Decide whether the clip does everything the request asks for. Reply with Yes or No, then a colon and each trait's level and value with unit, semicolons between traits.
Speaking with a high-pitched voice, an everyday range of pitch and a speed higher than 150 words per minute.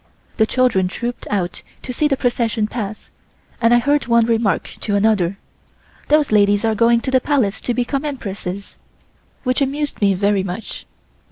Yes: high, 230 Hz; average, 3.9 semitones; average, 165 wpm